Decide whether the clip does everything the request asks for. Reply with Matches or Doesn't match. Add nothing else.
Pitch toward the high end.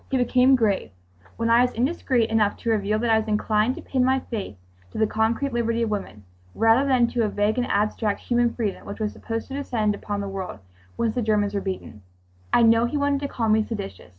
Matches